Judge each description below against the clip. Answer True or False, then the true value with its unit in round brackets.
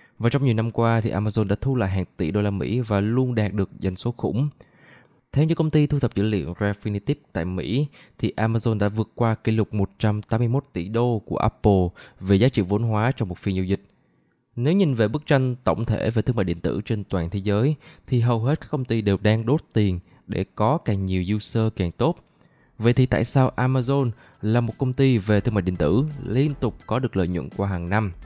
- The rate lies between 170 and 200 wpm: False (235 wpm)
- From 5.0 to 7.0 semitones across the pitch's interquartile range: False (4.2 semitones)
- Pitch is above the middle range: False (110 Hz)